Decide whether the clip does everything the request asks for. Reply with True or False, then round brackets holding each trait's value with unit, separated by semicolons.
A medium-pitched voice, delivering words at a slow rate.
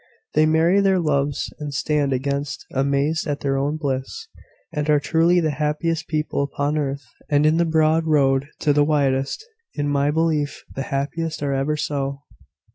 False (150 Hz; 170 wpm)